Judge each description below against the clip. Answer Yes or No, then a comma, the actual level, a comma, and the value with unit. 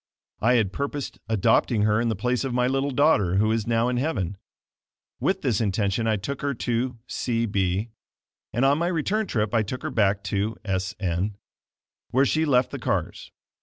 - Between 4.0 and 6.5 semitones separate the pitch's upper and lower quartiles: Yes, average, 4.3 semitones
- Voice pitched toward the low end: Yes, low, 115 Hz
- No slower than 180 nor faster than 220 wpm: Yes, average, 190 wpm